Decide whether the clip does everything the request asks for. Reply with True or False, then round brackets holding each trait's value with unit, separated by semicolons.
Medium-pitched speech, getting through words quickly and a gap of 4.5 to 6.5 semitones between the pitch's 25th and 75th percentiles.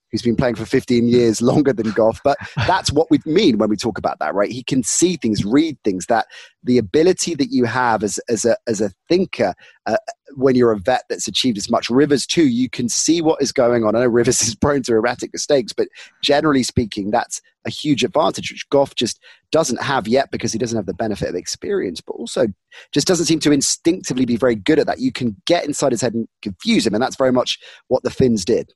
False (130 Hz; 240 wpm; 4.9 semitones)